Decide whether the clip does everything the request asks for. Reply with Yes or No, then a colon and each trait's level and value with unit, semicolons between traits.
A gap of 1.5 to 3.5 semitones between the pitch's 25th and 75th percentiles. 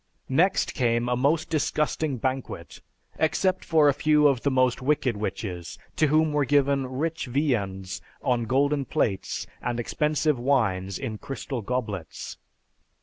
No: average, 4.1 semitones